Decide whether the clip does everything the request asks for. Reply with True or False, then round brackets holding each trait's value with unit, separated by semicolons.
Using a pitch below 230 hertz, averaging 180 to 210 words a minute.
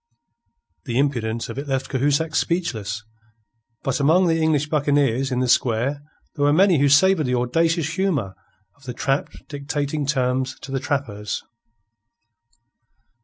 False (140 Hz; 140 wpm)